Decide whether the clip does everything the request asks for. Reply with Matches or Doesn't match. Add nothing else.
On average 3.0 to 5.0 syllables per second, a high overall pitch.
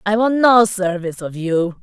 Matches